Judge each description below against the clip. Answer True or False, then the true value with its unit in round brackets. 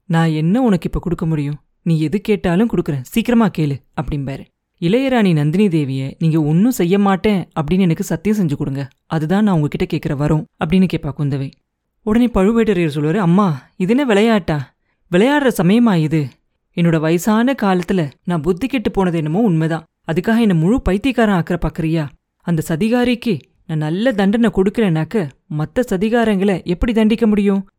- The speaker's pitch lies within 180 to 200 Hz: True (185 Hz)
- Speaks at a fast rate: True (145 wpm)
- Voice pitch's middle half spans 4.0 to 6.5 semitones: True (5.1 semitones)